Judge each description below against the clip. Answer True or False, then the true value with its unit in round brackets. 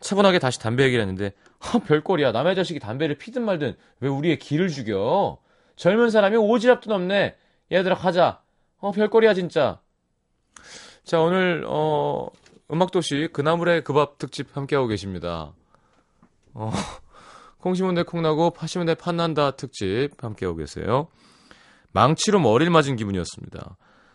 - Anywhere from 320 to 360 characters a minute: False (310 characters per minute)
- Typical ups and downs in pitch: False (5.9 semitones)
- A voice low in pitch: False (160 Hz)